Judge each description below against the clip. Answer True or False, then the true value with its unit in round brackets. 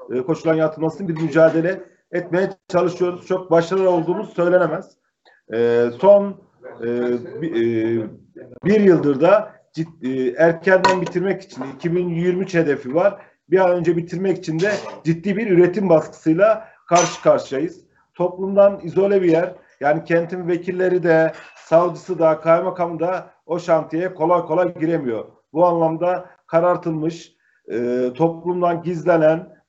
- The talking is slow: False (120 wpm)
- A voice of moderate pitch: True (175 Hz)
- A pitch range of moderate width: False (2.3 semitones)